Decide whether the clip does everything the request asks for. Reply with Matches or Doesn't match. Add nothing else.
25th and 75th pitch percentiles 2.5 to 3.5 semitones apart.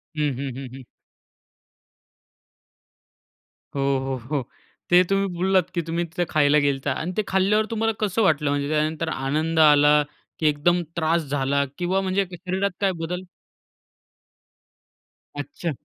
Doesn't match